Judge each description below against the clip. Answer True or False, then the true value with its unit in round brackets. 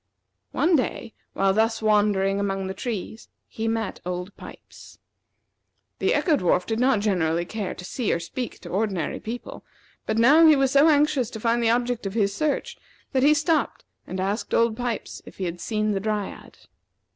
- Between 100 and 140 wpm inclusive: False (180 wpm)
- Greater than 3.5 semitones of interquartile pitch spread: True (4.2 semitones)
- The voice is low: False (220 Hz)